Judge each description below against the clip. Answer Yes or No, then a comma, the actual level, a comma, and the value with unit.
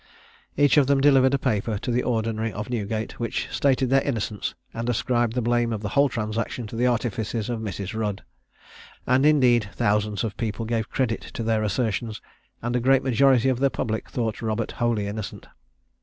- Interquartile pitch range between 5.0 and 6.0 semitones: No, average, 2.7 semitones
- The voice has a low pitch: Yes, low, 115 Hz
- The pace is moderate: Yes, average, 185 wpm